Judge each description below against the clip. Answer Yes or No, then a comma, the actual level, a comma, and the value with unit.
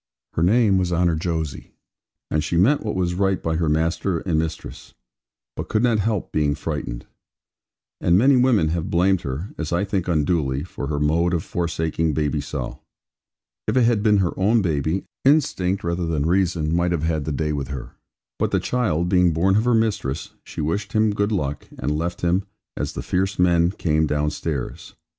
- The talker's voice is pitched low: Yes, very low, 85 Hz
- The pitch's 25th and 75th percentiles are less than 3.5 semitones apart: No, average, 3.9 semitones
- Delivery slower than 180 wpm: No, average, 190 wpm